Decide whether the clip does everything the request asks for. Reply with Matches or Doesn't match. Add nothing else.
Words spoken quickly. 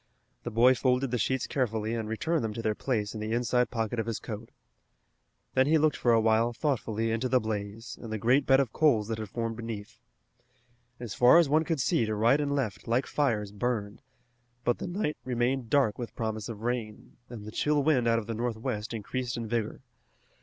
Matches